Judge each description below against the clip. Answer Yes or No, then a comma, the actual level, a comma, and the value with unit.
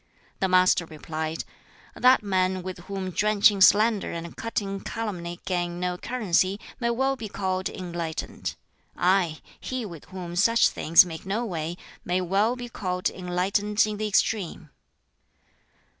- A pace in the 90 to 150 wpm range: Yes, average, 140 wpm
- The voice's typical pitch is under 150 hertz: No, medium, 185 Hz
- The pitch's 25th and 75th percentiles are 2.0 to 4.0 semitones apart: Yes, average, 3.2 semitones